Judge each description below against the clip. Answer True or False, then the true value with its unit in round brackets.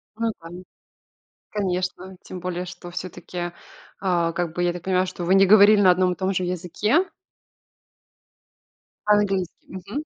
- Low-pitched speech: False (185 Hz)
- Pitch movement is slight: True (1.7 semitones)